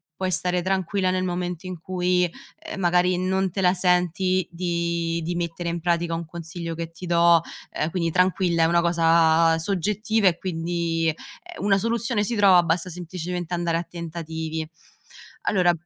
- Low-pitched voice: No, medium, 175 Hz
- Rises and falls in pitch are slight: Yes, narrow, 1.8 semitones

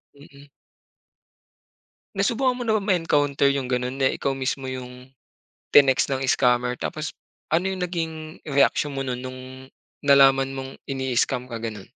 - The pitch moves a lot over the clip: No, average, 3.3 semitones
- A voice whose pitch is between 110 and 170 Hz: Yes, low, 135 Hz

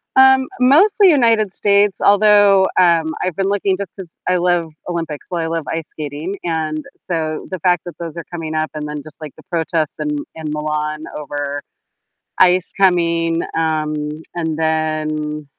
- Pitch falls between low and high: Yes, medium, 165 Hz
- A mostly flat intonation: No, average, 3.5 semitones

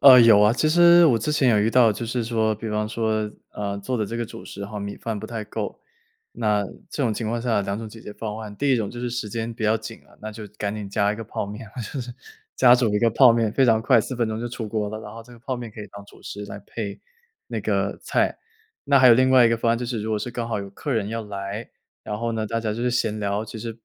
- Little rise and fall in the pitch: Yes, narrow, 2.1 semitones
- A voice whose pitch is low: Yes, low, 110 Hz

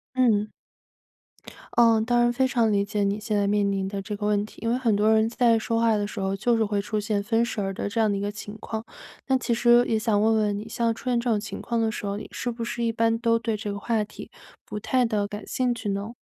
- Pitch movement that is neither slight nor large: No, narrow, 2.2 semitones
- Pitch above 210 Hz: Yes, high, 220 Hz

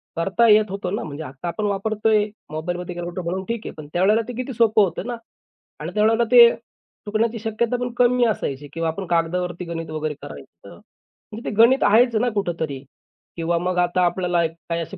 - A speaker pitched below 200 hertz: Yes, medium, 185 Hz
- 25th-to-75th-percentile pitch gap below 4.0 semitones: No, average, 4.8 semitones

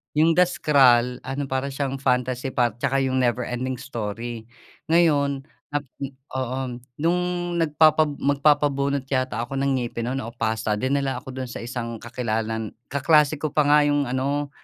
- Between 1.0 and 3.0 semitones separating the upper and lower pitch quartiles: Yes, average, 2.7 semitones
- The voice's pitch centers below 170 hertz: Yes, low, 135 Hz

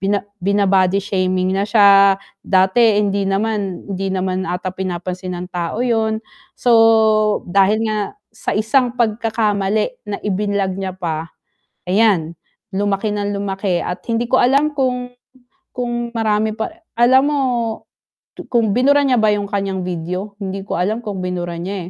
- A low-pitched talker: No, high, 200 Hz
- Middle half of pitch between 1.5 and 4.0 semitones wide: Yes, average, 2.9 semitones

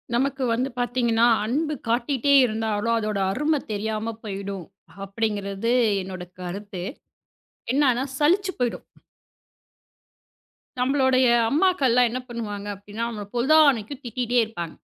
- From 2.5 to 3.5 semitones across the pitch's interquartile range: No, average, 4.2 semitones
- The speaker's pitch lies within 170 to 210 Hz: No, high, 230 Hz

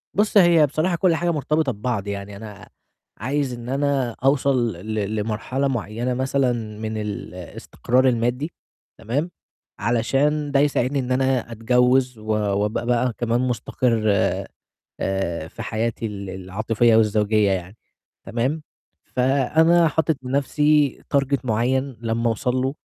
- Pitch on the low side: Yes, low, 125 Hz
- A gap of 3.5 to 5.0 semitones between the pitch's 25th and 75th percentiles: Yes, average, 4.2 semitones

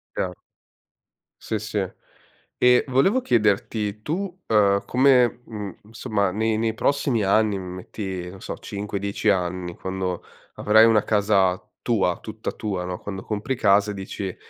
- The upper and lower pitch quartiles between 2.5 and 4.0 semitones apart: Yes, average, 2.8 semitones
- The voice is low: Yes, low, 105 Hz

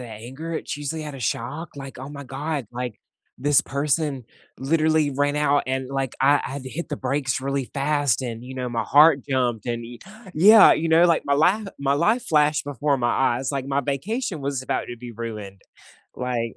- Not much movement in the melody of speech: No, average, 3.0 semitones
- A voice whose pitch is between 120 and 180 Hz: Yes, medium, 140 Hz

